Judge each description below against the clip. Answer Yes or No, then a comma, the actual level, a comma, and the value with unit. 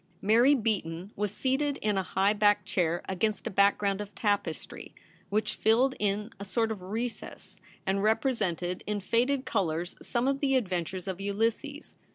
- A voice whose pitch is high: Yes, high, 205 Hz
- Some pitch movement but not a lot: Yes, average, 3.4 semitones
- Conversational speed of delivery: Yes, average, 160 wpm